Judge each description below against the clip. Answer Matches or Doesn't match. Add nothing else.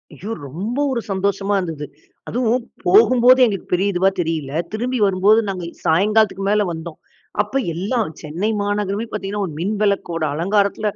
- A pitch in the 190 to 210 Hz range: Matches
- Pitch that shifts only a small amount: Doesn't match